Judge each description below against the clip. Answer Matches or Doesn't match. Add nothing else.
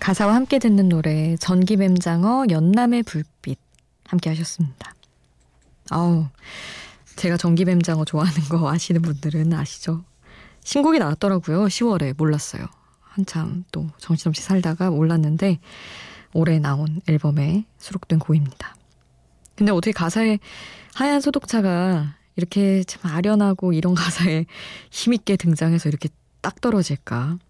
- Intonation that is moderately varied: Matches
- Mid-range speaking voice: Matches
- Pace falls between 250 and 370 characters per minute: Matches